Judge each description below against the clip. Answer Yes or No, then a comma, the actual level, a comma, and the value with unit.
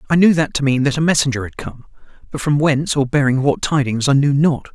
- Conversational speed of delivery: No, fast, 255 wpm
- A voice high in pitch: No, medium, 140 Hz